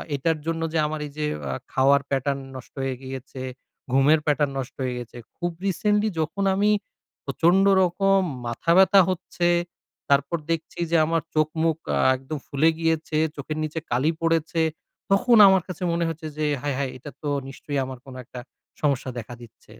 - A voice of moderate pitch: Yes, medium, 155 Hz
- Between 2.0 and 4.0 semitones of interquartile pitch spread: Yes, average, 3.7 semitones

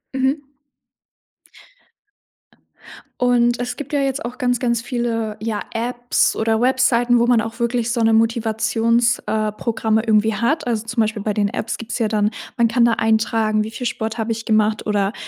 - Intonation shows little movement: Yes, narrow, 1.7 semitones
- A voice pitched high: Yes, high, 230 Hz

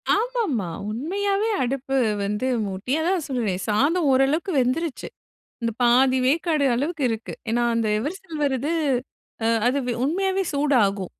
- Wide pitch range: Yes, wide, 5.9 semitones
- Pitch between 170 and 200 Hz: No, very high, 275 Hz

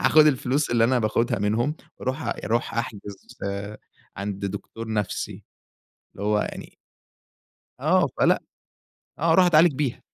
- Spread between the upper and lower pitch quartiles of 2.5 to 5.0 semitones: No, wide, 5.4 semitones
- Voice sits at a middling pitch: No, low, 115 Hz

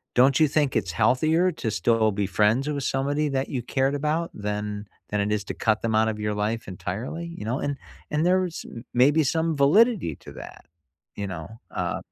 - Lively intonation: Yes, wide, 6.2 semitones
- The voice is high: No, low, 130 Hz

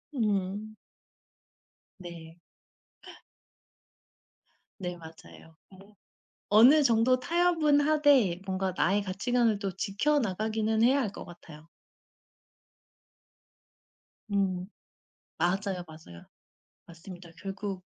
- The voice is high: Yes, high, 200 Hz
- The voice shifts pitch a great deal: No, average, 4.6 semitones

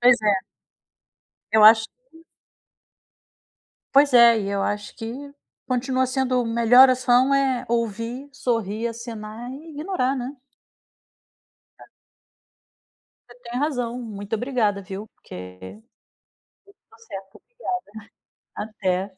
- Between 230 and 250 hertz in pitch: Yes, high, 235 Hz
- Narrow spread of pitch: No, average, 3.2 semitones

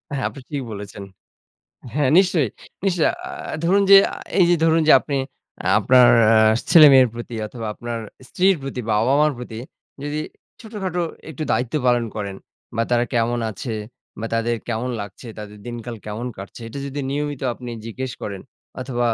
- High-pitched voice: No, low, 125 Hz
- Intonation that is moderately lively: Yes, average, 4.5 semitones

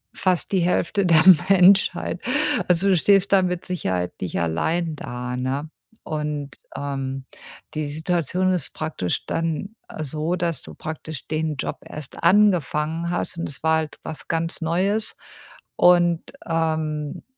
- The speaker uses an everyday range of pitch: Yes, average, 3.1 semitones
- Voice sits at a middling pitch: Yes, medium, 160 Hz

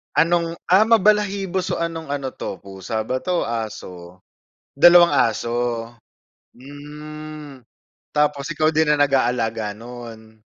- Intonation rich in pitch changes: Yes, wide, 6.2 semitones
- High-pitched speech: No, medium, 145 Hz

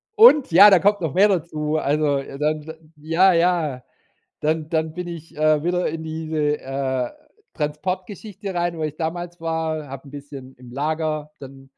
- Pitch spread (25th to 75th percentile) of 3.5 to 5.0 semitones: No, average, 2.8 semitones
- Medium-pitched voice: Yes, medium, 155 Hz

